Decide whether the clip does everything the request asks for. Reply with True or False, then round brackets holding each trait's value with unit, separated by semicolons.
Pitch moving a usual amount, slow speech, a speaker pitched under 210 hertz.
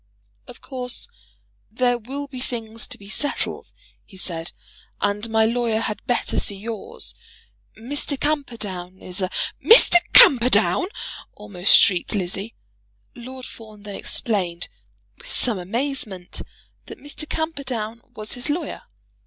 False (4.2 semitones; 130 wpm; 225 Hz)